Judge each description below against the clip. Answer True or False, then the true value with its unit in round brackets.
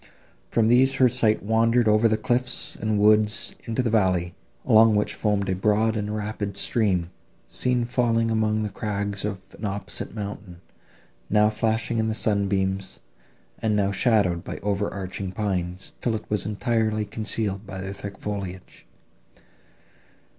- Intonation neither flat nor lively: False (2.1 semitones)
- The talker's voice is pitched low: True (105 Hz)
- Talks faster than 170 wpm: False (150 wpm)